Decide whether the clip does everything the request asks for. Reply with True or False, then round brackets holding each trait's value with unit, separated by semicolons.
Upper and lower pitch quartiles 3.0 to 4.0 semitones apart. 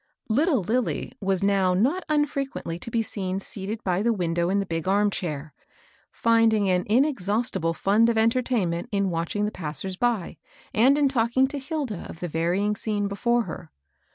False (4.4 semitones)